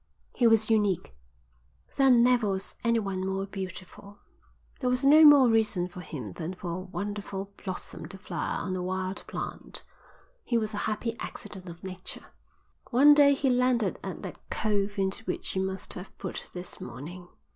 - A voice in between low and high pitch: No, high, 200 Hz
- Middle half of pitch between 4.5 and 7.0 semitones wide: No, average, 3.9 semitones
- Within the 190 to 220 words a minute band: No, average, 165 wpm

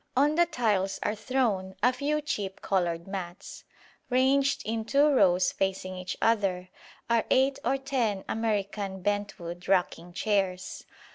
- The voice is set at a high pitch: Yes, high, 205 Hz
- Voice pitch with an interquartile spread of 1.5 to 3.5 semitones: No, wide, 5.5 semitones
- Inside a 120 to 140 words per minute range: Yes, slow, 135 wpm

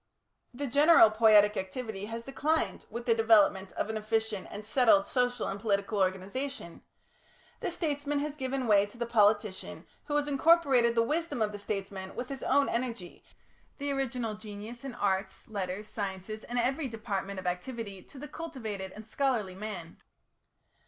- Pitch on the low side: No, high, 225 Hz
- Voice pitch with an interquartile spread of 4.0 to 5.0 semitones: Yes, average, 4.7 semitones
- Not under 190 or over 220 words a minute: No, average, 160 wpm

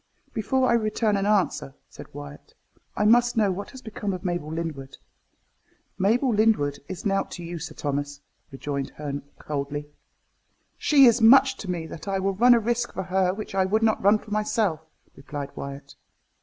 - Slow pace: No, average, 185 wpm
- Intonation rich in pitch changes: Yes, wide, 6.7 semitones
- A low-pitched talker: No, high, 195 Hz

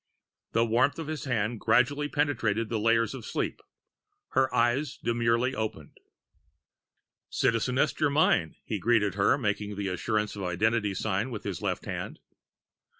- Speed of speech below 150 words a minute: Yes, average, 140 wpm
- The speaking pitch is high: No, low, 115 Hz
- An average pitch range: Yes, average, 3.7 semitones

